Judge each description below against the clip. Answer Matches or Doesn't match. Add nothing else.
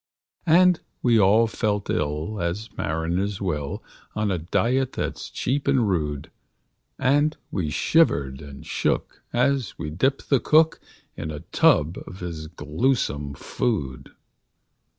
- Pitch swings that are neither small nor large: Doesn't match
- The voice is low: Matches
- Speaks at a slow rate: Matches